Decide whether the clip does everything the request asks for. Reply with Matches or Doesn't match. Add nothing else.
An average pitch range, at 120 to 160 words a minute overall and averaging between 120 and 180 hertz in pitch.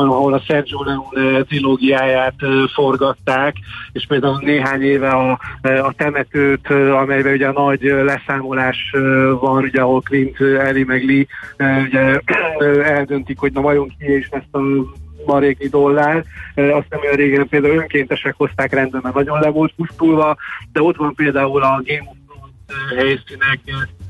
Doesn't match